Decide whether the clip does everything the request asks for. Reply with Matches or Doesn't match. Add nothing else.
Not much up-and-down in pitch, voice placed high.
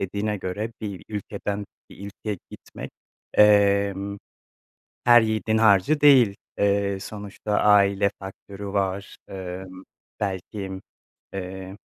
Doesn't match